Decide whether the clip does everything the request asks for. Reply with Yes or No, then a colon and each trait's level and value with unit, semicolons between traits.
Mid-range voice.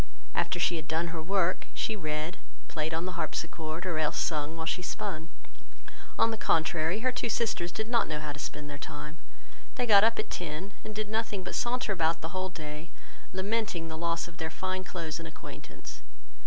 Yes: medium, 170 Hz